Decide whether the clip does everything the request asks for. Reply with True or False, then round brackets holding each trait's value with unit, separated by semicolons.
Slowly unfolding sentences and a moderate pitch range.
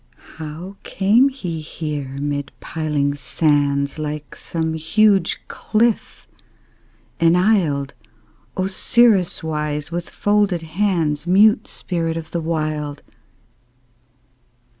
True (90 wpm; 4.3 semitones)